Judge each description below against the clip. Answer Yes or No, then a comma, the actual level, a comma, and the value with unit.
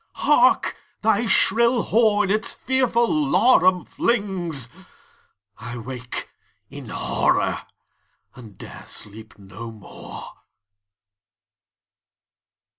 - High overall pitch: Yes, high, 195 Hz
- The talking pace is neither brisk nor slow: No, slow, 80 wpm